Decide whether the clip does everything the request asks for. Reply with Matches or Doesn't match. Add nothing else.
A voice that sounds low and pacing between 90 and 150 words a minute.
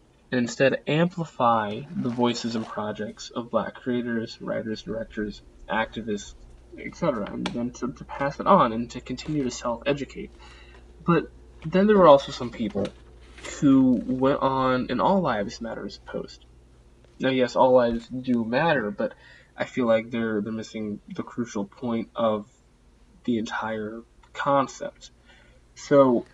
Matches